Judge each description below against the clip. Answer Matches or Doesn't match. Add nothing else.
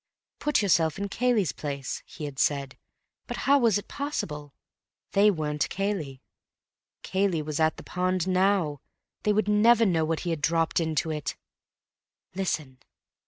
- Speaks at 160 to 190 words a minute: Doesn't match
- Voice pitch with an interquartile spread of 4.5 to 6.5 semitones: Matches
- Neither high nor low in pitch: Matches